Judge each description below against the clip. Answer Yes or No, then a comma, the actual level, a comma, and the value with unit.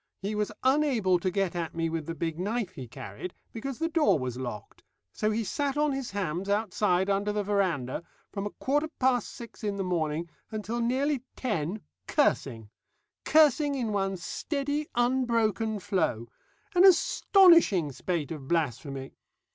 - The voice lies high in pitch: Yes, high, 205 Hz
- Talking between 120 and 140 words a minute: No, average, 155 wpm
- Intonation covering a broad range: Yes, wide, 7.4 semitones